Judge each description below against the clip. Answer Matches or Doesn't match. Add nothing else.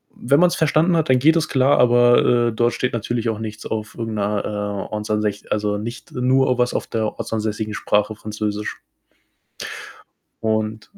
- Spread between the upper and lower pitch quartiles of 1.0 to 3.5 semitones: Matches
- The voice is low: Matches